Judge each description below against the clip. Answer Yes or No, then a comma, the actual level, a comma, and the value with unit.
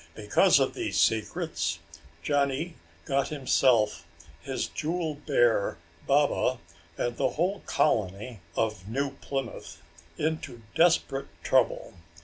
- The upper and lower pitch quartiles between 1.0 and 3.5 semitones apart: No, average, 5.2 semitones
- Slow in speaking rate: Yes, slow, 105 wpm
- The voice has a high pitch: No, low, 135 Hz